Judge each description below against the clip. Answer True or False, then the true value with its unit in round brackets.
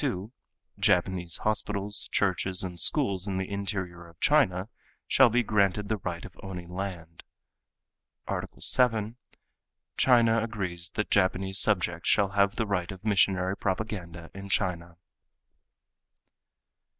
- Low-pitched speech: True (95 Hz)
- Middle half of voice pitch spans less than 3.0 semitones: True (2.6 semitones)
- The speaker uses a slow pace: True (125 wpm)